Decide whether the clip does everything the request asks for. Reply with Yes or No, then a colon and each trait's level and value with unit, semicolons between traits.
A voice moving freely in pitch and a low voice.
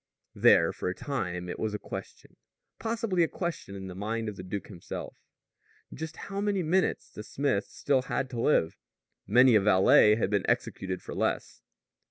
Yes: wide, 8.3 semitones; low, 110 Hz